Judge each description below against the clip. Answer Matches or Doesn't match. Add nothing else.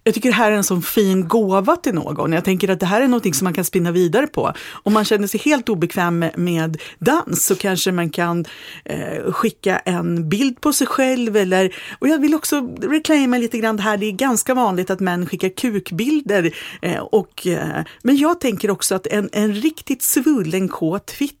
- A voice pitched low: Doesn't match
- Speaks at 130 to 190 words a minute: Doesn't match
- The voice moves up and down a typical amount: Doesn't match